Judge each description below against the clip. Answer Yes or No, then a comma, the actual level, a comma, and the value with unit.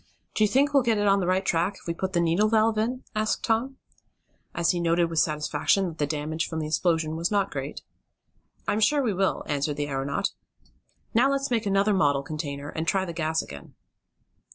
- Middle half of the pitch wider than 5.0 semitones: Yes, wide, 5.5 semitones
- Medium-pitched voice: Yes, medium, 175 Hz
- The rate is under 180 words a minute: No, fast, 205 wpm